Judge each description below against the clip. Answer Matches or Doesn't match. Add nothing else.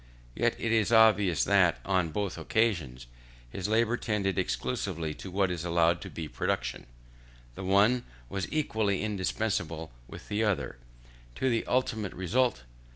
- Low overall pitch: Matches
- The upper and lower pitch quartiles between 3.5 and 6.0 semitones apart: Matches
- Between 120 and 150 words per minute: Matches